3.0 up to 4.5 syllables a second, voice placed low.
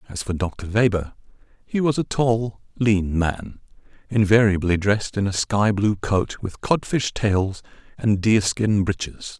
Yes: 4.0 syllables/s; low, 105 Hz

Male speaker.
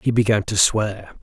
Yes: male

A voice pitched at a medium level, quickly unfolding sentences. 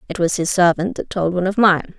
Yes: medium, 180 Hz; fast, 270 wpm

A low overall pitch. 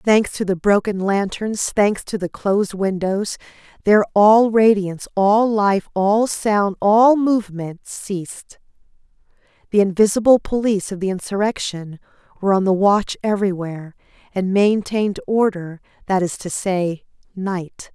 No: high, 200 Hz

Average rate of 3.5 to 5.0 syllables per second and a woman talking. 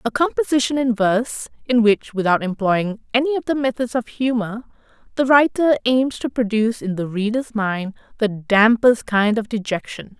Yes: 4.9 syllables/s; female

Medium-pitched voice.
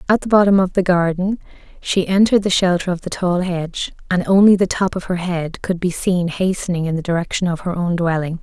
Yes: medium, 180 Hz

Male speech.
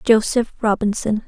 No: female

